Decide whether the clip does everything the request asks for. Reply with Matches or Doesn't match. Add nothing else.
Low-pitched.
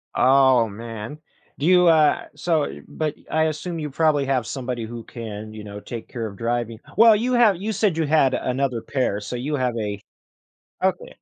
Matches